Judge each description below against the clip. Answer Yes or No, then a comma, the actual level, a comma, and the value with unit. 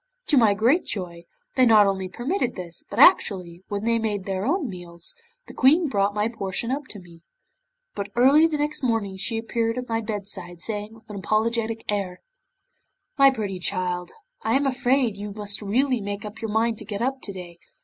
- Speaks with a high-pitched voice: Yes, high, 215 Hz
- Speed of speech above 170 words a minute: Yes, average, 195 wpm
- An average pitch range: Yes, average, 3.9 semitones